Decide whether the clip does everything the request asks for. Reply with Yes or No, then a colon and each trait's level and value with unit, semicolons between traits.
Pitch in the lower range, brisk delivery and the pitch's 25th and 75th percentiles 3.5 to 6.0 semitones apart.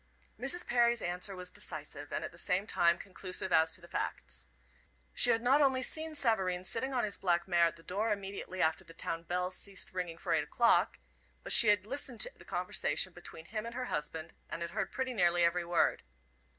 No: medium, 185 Hz; fast, 210 wpm; wide, 5.4 semitones